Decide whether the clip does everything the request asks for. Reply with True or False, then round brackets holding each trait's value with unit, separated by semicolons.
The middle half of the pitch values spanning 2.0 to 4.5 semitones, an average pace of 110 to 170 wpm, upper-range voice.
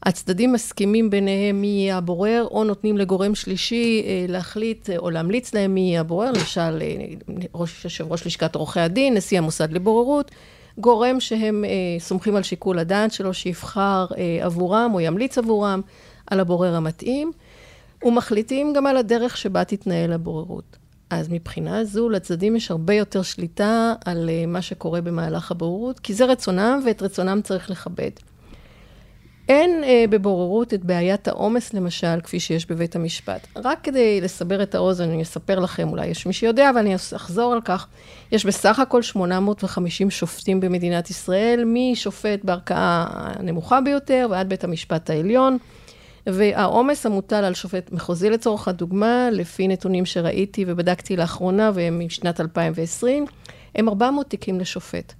True (4.2 semitones; 145 wpm; 195 Hz)